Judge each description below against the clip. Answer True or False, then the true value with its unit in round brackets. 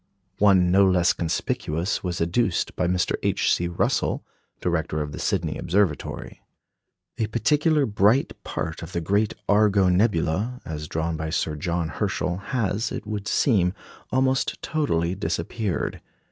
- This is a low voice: True (90 Hz)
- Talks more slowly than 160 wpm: True (140 wpm)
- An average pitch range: True (4.2 semitones)